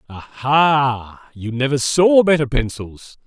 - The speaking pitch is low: Yes, low, 130 Hz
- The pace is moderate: No, slow, 110 wpm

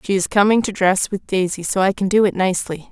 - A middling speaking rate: No, fast, 270 wpm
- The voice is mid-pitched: No, high, 195 Hz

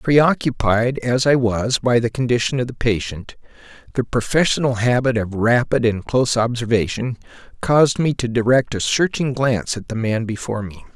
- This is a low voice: Yes, low, 120 Hz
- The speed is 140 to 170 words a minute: Yes, average, 165 wpm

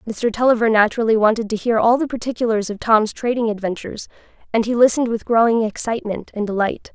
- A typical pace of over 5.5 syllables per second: Yes, 6.5 syllables/s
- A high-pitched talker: Yes, high, 225 Hz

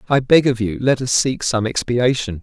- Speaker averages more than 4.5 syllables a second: Yes, 5.0 syllables/s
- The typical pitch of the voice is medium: No, low, 120 Hz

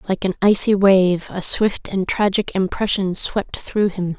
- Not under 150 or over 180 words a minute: Yes, average, 170 wpm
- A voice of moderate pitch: No, high, 195 Hz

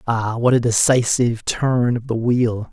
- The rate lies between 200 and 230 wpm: No, average, 175 wpm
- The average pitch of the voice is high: No, low, 120 Hz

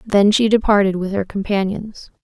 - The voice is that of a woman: Yes, female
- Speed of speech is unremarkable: Yes, average, 160 wpm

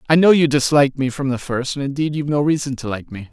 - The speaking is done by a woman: No, male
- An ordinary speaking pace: No, fast, 290 wpm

